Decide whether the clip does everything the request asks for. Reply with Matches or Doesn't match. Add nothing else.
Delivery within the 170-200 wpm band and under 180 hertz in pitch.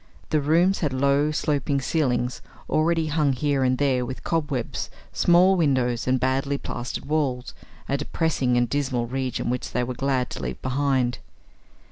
Doesn't match